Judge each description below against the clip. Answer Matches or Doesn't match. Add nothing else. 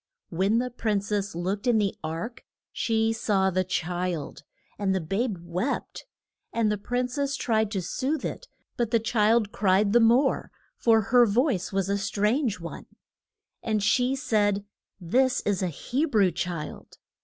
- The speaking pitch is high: Matches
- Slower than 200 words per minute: Matches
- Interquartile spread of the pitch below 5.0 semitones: Matches